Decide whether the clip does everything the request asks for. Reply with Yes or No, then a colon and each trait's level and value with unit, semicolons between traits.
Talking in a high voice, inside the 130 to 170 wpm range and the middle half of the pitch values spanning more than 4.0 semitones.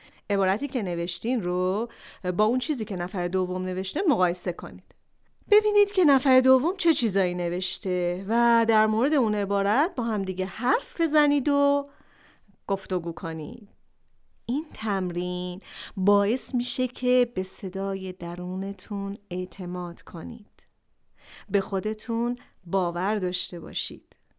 No: high, 200 Hz; average, 115 wpm; average, 5.2 semitones